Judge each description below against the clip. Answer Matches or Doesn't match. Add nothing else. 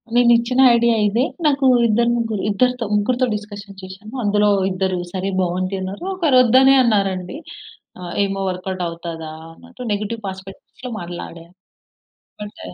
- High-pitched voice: Matches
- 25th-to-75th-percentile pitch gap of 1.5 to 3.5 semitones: Doesn't match